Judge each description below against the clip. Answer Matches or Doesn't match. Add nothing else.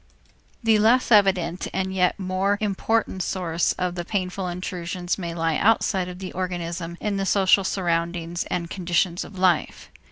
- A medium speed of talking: Matches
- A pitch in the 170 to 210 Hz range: Matches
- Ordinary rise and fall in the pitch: Doesn't match